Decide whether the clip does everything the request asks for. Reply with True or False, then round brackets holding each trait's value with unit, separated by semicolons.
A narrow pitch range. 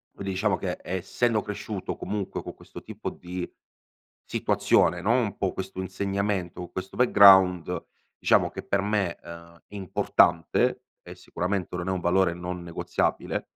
True (2.1 semitones)